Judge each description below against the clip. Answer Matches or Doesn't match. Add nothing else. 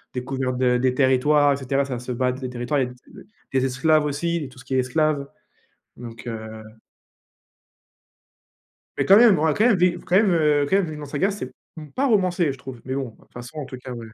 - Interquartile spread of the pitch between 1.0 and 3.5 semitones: Doesn't match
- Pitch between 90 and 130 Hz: Doesn't match